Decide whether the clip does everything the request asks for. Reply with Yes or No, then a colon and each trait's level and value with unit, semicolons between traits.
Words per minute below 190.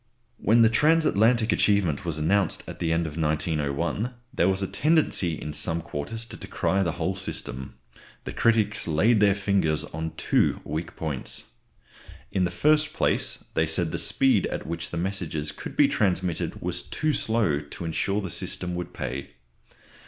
Yes: average, 170 wpm